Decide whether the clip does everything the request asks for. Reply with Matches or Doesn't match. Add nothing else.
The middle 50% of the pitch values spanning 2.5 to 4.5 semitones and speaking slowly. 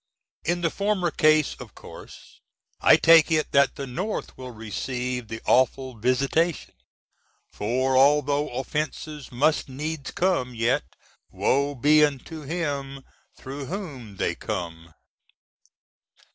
Matches